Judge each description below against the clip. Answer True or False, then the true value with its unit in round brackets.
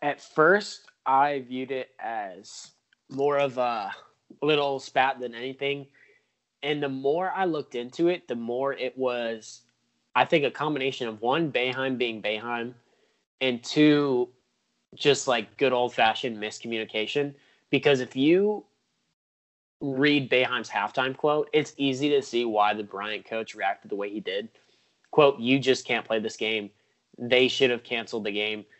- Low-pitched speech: True (130 Hz)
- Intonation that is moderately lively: True (3.6 semitones)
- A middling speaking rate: True (150 wpm)